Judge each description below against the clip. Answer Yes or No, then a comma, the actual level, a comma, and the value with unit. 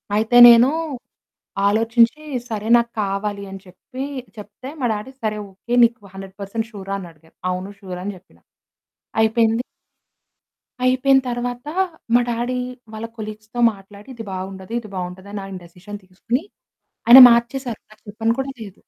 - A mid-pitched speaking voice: No, high, 215 Hz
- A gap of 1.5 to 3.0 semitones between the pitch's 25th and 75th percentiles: No, average, 3.4 semitones